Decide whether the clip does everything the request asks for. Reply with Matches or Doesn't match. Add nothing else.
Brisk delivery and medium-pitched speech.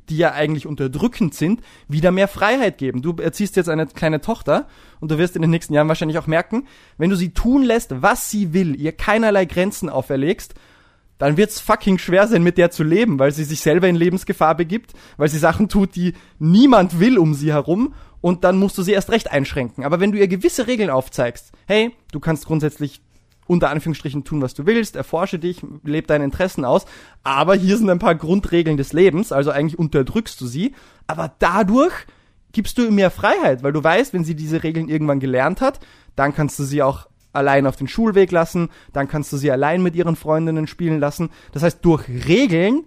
Matches